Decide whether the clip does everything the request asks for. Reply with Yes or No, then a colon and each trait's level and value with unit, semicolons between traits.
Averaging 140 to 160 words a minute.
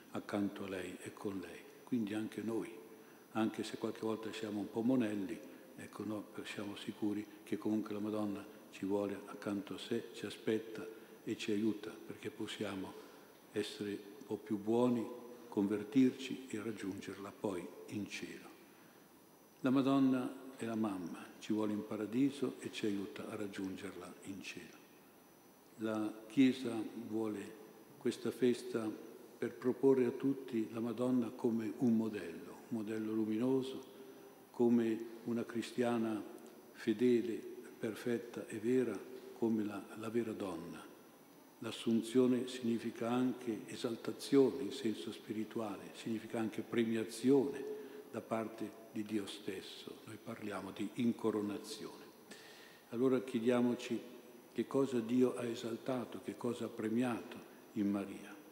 No: average, 130 wpm